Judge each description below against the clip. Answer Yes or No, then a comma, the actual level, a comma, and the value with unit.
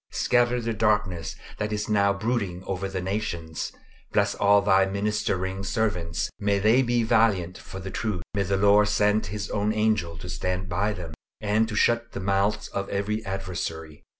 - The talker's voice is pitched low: Yes, low, 100 Hz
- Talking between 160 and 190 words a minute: Yes, average, 175 wpm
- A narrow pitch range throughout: Yes, narrow, 2.2 semitones